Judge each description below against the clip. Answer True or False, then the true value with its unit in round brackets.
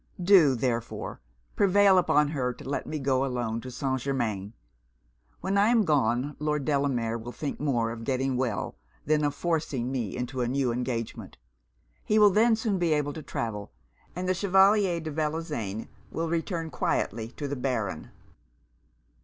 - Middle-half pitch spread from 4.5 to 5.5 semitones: True (5.2 semitones)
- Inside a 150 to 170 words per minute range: True (160 wpm)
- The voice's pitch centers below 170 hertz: True (140 Hz)